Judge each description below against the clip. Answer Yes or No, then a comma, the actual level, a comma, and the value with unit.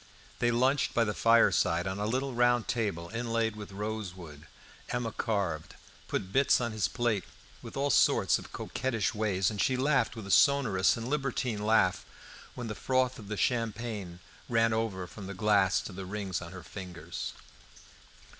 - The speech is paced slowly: No, average, 170 wpm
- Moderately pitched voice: No, low, 110 Hz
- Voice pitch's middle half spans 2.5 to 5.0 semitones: Yes, average, 3.9 semitones